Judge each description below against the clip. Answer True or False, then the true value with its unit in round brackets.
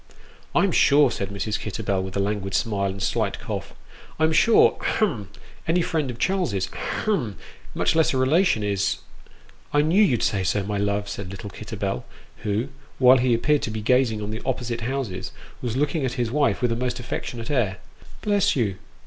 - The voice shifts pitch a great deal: True (6.0 semitones)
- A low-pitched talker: True (120 Hz)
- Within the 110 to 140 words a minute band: False (200 wpm)